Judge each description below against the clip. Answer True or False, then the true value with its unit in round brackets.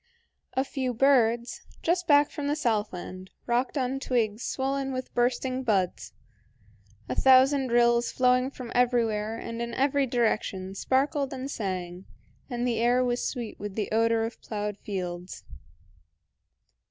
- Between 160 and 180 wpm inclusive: False (140 wpm)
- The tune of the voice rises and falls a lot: False (3.5 semitones)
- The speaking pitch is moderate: False (240 Hz)